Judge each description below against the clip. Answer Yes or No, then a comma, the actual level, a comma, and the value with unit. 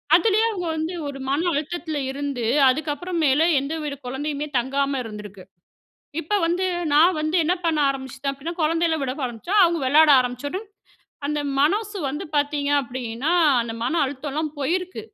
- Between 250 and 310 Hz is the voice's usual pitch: Yes, very high, 290 Hz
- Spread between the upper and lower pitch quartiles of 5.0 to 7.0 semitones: No, average, 3.7 semitones